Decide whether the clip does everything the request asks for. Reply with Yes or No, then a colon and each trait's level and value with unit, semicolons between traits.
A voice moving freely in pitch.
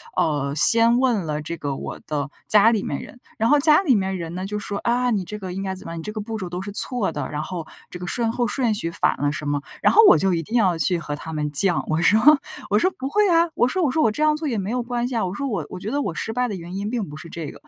Yes: wide, 6.3 semitones